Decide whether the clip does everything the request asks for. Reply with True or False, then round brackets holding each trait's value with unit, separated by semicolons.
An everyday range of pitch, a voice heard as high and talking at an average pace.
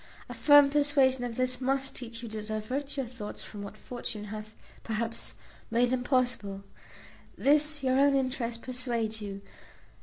True (3.5 semitones; 245 Hz; 150 wpm)